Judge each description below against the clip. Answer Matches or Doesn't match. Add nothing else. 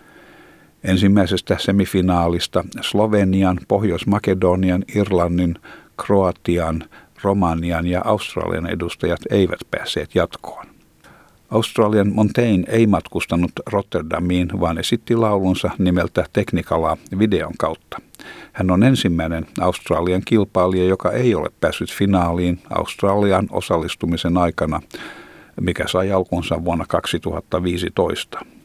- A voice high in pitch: Doesn't match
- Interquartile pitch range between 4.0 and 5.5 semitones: Doesn't match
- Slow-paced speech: Matches